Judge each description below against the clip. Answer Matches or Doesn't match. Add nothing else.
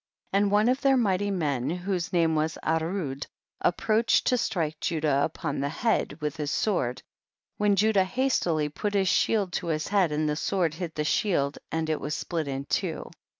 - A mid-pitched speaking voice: Matches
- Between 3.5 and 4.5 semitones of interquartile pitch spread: Doesn't match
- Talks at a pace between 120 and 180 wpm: Doesn't match